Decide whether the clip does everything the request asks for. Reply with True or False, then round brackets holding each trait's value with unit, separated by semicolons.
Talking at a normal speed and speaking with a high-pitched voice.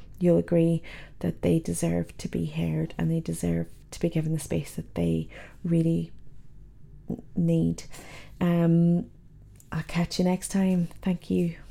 False (145 wpm; 160 Hz)